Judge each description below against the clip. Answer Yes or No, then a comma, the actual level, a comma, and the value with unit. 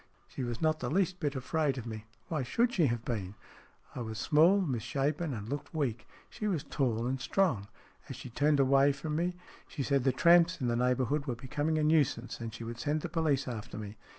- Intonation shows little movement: No, average, 4.6 semitones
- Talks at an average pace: No, fast, 215 wpm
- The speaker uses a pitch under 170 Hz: Yes, medium, 140 Hz